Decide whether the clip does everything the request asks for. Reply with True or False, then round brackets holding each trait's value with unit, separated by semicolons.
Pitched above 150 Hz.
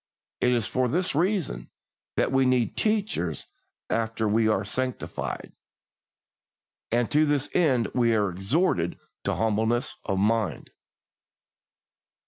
False (120 Hz)